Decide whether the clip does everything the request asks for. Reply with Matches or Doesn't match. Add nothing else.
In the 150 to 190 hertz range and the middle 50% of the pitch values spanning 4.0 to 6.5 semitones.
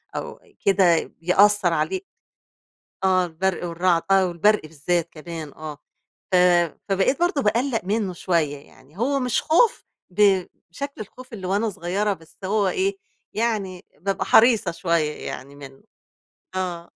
Matches